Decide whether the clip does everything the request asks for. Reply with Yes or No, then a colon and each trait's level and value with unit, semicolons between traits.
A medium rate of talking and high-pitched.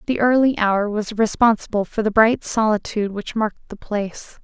Yes: average, 175 wpm; high, 215 Hz